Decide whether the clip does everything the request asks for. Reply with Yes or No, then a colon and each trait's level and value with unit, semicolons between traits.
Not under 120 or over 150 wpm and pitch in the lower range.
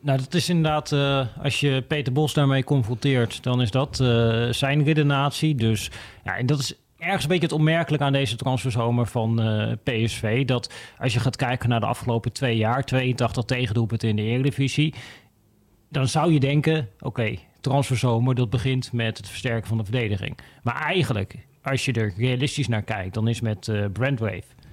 No: average, 185 wpm; low, 125 Hz